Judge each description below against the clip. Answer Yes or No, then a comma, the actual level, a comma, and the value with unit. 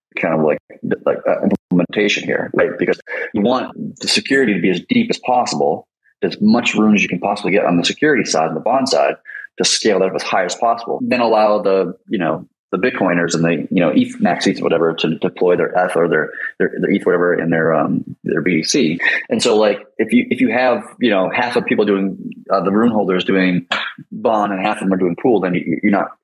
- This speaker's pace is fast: Yes, fast, 240 wpm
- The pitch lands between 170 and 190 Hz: No, low, 105 Hz